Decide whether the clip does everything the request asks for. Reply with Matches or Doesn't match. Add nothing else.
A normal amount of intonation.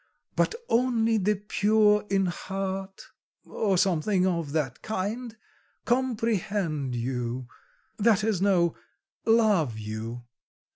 Doesn't match